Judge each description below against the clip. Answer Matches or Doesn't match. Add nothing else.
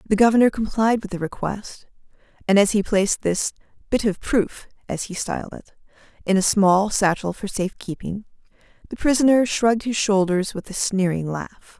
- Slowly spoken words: Doesn't match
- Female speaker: Matches